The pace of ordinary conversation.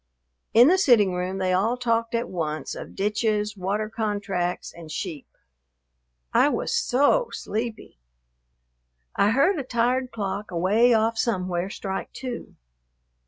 No: slow, 130 wpm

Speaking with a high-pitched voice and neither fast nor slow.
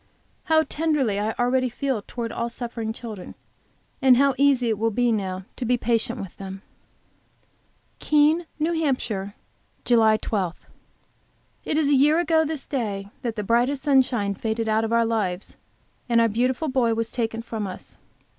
Yes: high, 235 Hz; average, 165 wpm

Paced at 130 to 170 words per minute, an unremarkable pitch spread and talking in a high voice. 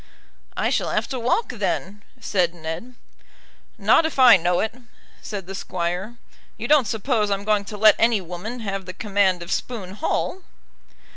Yes: average, 165 wpm; average, 4.1 semitones; high, 205 Hz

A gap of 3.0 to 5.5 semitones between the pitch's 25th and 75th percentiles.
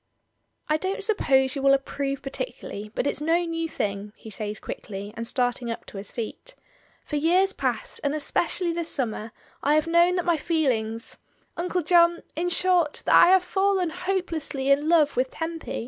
Yes: average, 5.2 semitones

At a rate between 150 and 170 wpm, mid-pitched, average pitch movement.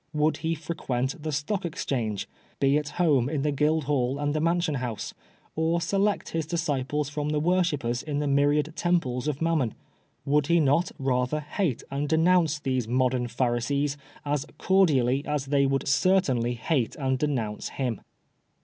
Yes: average, 165 wpm; medium, 145 Hz; average, 3.4 semitones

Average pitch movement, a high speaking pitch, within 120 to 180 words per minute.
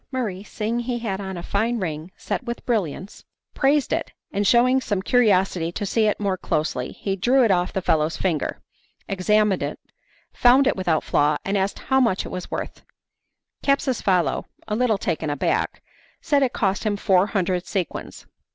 Yes: average, 4.6 semitones; high, 200 Hz; average, 175 wpm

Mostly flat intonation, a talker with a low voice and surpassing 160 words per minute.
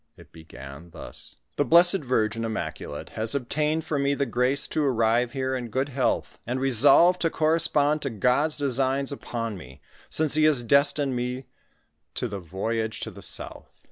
No: average, 4.2 semitones; low, 130 Hz; average, 180 wpm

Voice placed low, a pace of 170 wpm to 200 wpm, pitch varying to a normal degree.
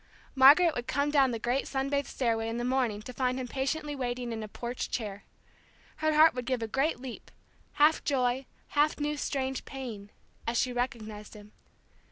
No: very high, 255 Hz; average, 190 wpm; average, 3.1 semitones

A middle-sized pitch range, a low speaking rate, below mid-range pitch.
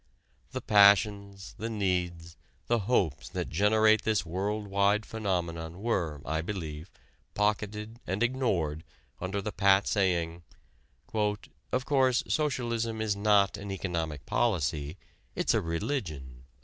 Yes: average, 4.4 semitones; slow, 120 wpm; low, 100 Hz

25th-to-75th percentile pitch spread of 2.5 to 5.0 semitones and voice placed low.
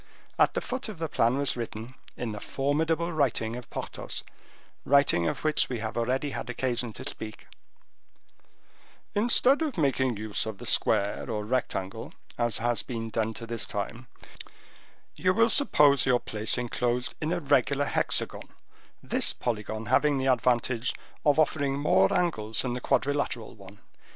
Yes: average, 4.2 semitones; low, 125 Hz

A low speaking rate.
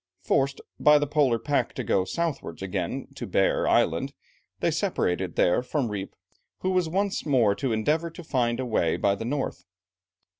No: average, 175 wpm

